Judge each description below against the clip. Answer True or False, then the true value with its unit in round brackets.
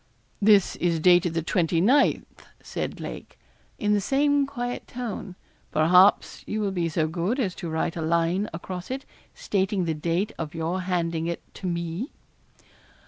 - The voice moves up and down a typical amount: True (3.8 semitones)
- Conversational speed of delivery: True (155 wpm)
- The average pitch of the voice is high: False (180 Hz)